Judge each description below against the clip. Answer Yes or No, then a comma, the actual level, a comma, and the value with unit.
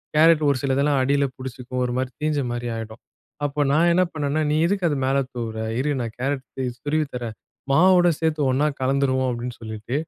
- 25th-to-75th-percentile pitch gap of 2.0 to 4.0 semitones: Yes, average, 3.4 semitones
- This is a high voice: No, medium, 140 Hz